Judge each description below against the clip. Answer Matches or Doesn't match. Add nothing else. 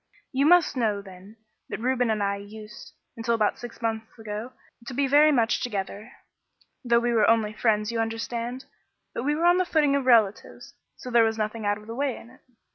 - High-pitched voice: Matches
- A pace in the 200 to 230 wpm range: Matches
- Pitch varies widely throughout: Doesn't match